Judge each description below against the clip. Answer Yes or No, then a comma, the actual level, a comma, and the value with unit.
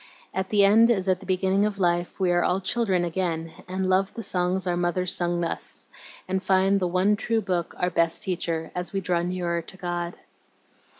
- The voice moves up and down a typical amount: No, narrow, 1.6 semitones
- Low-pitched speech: No, medium, 185 Hz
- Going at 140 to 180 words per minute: No, average, 200 wpm